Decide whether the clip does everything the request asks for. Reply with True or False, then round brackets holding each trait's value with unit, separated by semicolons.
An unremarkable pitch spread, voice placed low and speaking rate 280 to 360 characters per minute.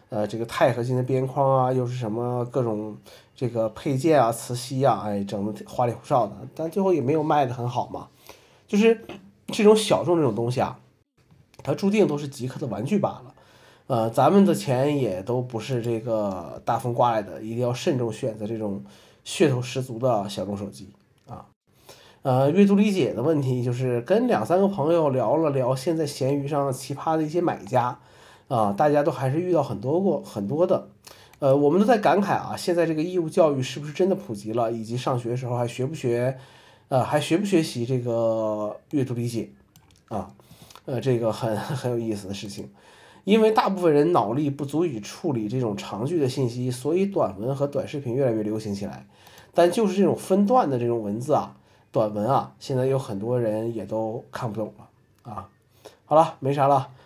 True (4.8 semitones; 130 Hz; 290 characters per minute)